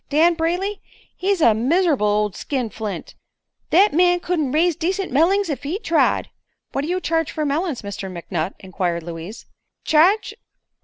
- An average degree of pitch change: No, wide, 8.8 semitones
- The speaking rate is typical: Yes, average, 150 wpm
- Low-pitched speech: No, very high, 310 Hz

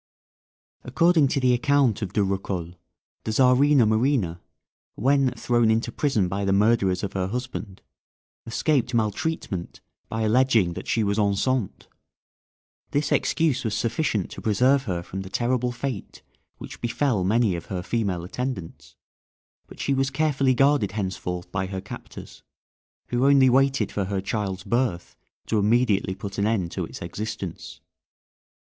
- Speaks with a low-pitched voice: Yes, low, 110 Hz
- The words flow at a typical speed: Yes, average, 145 wpm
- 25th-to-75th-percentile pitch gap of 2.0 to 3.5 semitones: No, average, 5.1 semitones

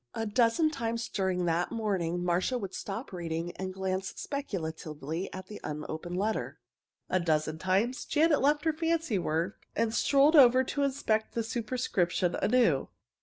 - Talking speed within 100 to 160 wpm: Yes, average, 150 wpm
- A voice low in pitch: No, high, 200 Hz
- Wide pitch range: Yes, wide, 6.4 semitones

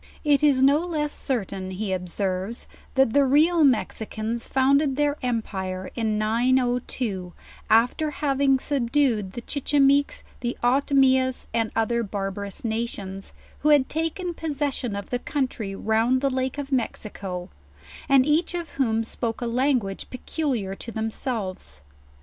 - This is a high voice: Yes, high, 245 Hz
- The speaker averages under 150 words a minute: Yes, slow, 135 wpm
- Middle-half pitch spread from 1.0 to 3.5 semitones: No, average, 4.5 semitones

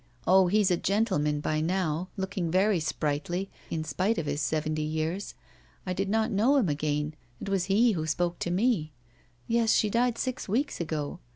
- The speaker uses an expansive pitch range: No, average, 4.8 semitones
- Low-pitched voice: No, medium, 180 Hz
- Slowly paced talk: No, average, 180 wpm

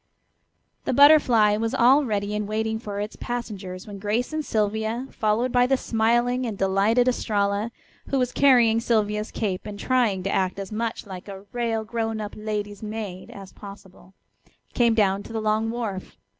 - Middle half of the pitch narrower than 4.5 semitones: Yes, narrow, 2.6 semitones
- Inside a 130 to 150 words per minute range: No, average, 170 wpm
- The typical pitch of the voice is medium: No, high, 215 Hz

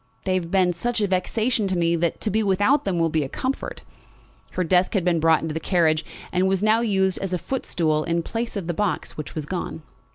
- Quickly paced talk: Yes, fast, 245 wpm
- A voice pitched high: No, medium, 180 Hz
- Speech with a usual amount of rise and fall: Yes, average, 3.4 semitones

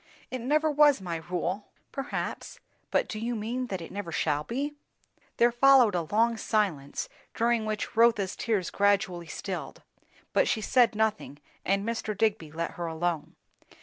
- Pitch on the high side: Yes, high, 215 Hz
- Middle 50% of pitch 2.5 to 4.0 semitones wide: No, average, 5.1 semitones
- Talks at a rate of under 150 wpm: No, average, 155 wpm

